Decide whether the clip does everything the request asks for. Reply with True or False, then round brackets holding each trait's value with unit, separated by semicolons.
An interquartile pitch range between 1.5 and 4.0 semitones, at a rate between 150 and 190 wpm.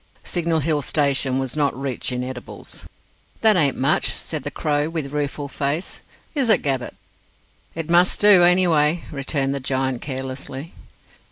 True (3.5 semitones; 155 wpm)